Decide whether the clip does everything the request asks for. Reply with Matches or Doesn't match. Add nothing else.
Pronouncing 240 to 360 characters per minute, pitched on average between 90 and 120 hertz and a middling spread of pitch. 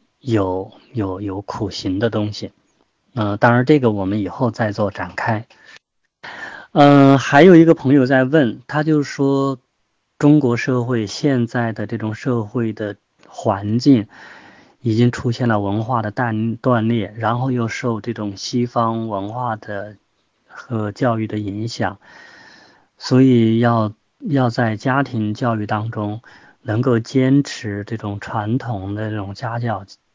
Doesn't match